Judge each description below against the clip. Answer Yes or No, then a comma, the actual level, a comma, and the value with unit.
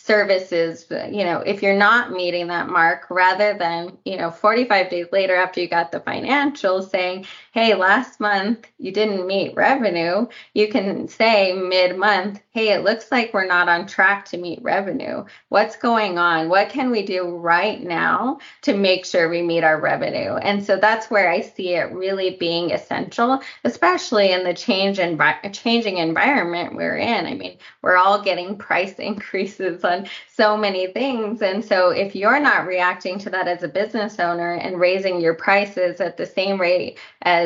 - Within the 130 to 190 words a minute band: Yes, average, 180 wpm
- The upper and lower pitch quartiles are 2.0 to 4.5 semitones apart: Yes, average, 2.9 semitones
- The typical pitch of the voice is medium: No, high, 195 Hz